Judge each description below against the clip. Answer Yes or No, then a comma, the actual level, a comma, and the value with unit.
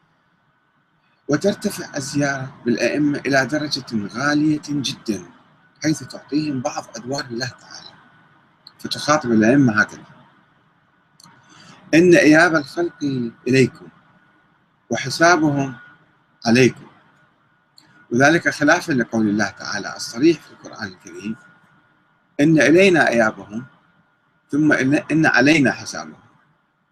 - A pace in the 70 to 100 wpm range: Yes, average, 85 wpm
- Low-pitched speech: No, medium, 145 Hz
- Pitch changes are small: No, average, 3.5 semitones